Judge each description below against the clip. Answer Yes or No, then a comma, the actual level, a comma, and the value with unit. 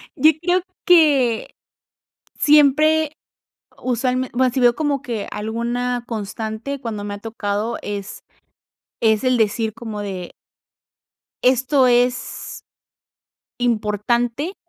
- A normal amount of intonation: Yes, average, 3.6 semitones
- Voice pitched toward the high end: Yes, high, 240 Hz